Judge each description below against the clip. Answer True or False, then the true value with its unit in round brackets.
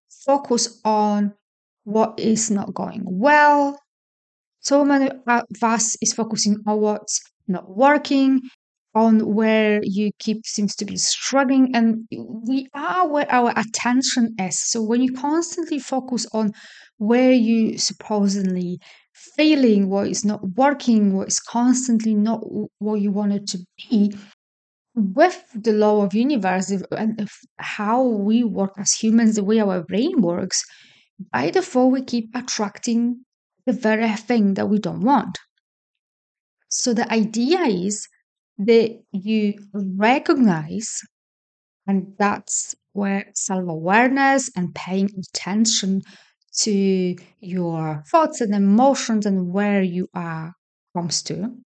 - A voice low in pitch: False (220 Hz)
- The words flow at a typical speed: False (125 wpm)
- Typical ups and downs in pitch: True (3.4 semitones)